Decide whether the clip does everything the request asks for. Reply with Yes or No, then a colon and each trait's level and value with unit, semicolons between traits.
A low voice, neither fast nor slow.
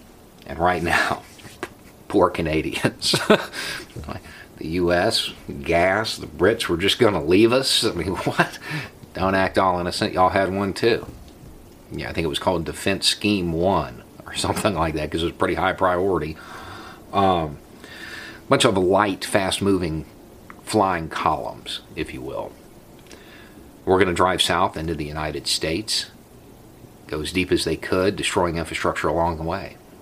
Yes: very low, 90 Hz; average, 150 wpm